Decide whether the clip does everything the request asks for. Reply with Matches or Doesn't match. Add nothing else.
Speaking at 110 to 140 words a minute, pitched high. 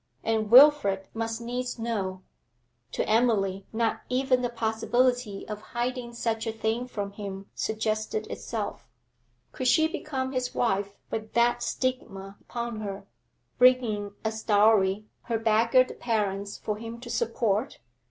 Matches